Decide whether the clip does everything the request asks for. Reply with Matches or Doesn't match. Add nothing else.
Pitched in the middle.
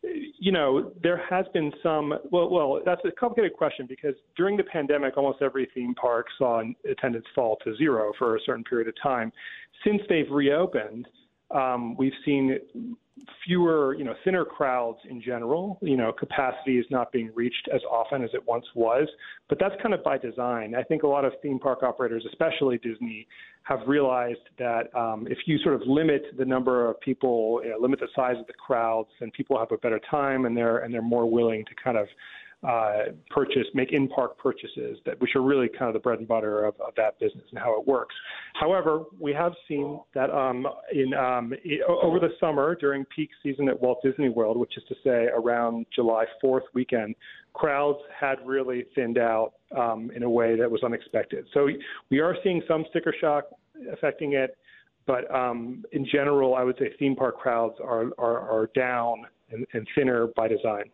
Doesn't match